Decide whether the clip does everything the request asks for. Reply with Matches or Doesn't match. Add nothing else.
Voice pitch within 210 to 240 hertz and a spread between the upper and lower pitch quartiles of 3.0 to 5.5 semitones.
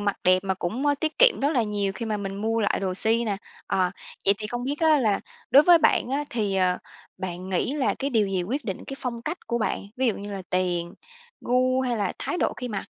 Matches